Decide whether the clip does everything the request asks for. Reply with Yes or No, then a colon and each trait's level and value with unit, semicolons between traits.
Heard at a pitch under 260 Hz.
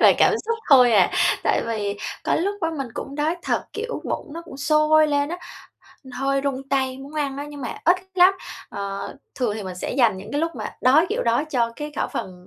No: very high, 275 Hz